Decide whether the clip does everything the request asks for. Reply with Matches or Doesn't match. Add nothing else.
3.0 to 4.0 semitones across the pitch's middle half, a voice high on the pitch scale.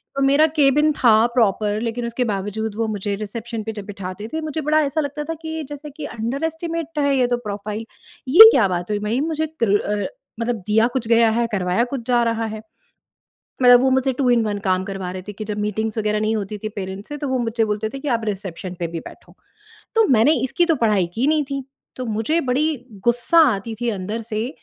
Doesn't match